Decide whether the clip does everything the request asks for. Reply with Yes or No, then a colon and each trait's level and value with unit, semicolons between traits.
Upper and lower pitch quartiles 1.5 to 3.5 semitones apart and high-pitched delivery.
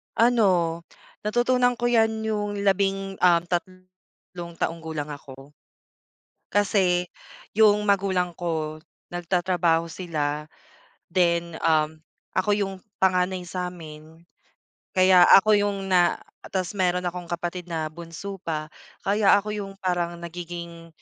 No: average, 2.8 semitones; medium, 180 Hz